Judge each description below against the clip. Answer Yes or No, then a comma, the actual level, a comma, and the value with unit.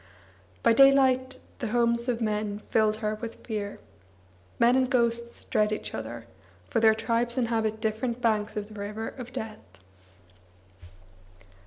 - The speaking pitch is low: No, high, 225 Hz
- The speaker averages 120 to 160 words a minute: Yes, average, 140 wpm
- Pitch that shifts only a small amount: Yes, narrow, 2.0 semitones